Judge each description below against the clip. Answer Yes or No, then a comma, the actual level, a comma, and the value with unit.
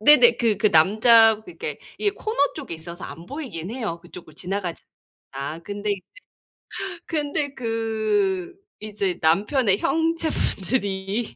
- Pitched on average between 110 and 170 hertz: No, high, 220 Hz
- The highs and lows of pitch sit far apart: Yes, wide, 7.3 semitones